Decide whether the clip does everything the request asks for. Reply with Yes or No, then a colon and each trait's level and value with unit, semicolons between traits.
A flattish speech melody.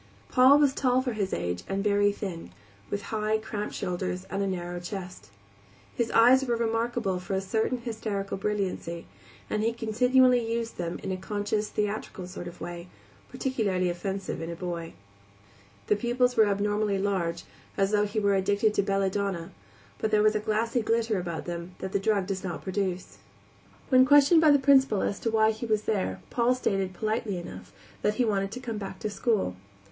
No: average, 3.3 semitones